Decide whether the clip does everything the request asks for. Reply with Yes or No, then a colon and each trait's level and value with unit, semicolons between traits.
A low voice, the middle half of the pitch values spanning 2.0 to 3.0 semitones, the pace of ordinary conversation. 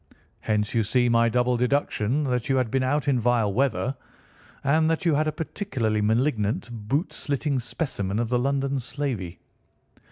No: low, 125 Hz; average, 3.8 semitones; average, 165 wpm